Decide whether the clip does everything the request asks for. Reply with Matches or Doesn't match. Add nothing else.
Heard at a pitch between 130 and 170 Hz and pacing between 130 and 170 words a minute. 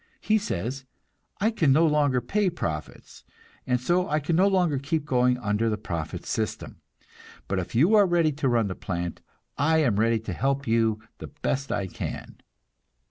Doesn't match